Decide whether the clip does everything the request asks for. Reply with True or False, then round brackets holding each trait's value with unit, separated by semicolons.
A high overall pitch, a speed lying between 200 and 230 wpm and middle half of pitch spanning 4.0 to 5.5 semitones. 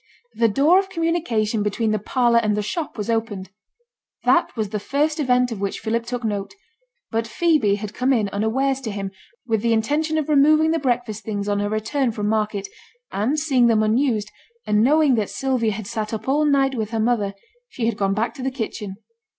True (230 Hz; 205 wpm; 4.3 semitones)